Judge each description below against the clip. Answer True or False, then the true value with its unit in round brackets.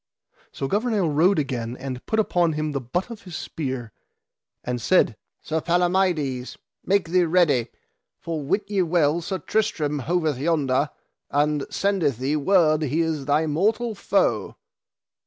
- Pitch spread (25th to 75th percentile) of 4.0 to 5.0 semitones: True (4.4 semitones)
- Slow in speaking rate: False (145 wpm)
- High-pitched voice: False (160 Hz)